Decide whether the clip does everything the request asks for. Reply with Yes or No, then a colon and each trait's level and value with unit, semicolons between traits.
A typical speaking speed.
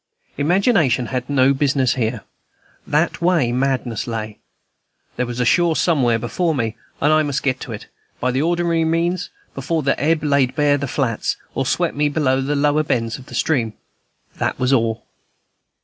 Yes: average, 175 wpm